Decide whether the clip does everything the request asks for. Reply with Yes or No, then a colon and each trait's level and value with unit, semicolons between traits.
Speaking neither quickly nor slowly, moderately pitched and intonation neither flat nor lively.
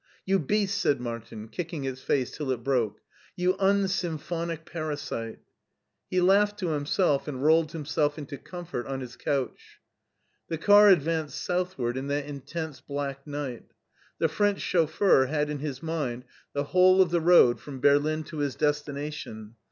Yes: average, 160 wpm; medium, 150 Hz; average, 4.1 semitones